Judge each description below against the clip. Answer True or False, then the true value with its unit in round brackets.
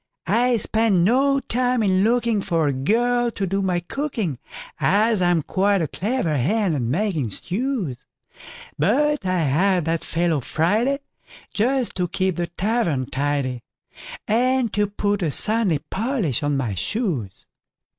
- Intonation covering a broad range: True (6.5 semitones)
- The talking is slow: True (125 wpm)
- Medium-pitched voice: False (195 Hz)